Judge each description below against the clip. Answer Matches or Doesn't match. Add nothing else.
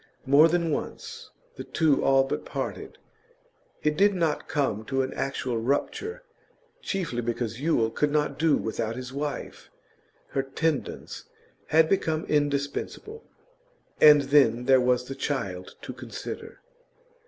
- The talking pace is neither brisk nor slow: Doesn't match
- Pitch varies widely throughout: Doesn't match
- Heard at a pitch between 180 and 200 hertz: Doesn't match